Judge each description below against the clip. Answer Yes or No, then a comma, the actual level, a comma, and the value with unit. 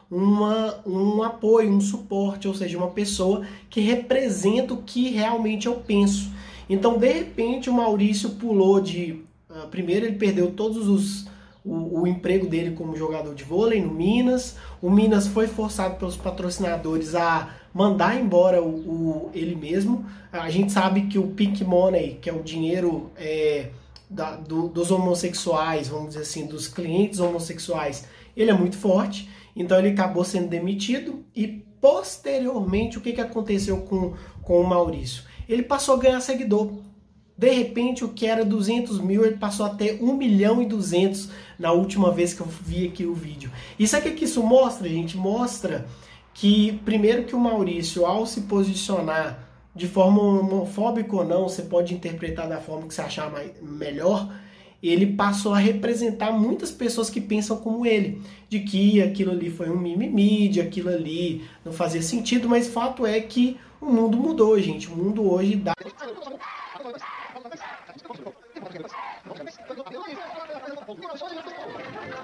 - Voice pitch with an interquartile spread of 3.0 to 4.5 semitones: Yes, average, 4.1 semitones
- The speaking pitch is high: Yes, high, 200 Hz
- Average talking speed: Yes, average, 155 wpm